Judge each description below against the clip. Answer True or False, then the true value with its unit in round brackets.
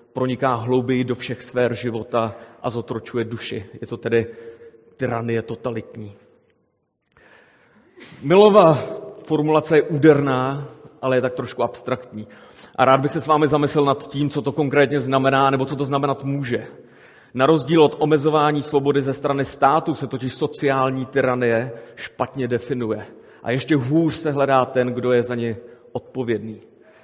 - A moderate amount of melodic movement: True (3.3 semitones)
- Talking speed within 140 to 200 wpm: True (145 wpm)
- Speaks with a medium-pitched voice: False (130 Hz)